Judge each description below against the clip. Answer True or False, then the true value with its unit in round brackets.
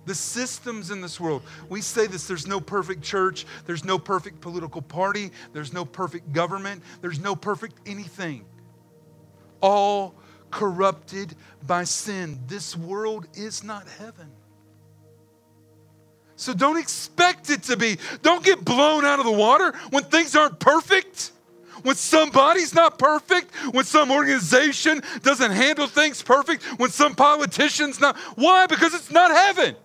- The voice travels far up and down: True (8.7 semitones)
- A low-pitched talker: False (210 Hz)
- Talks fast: False (145 wpm)